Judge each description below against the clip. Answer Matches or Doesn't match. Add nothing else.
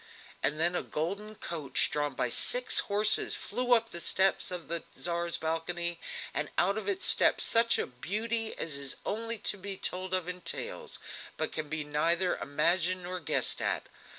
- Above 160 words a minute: Matches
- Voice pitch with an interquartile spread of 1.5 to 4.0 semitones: Doesn't match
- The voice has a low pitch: Doesn't match